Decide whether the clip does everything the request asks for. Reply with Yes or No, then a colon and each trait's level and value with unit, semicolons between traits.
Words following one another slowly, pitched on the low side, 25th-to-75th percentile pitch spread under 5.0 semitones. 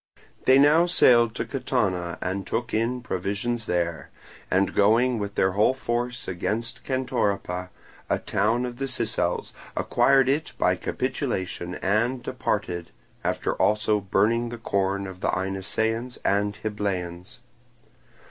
Yes: slow, 130 wpm; low, 110 Hz; average, 4.2 semitones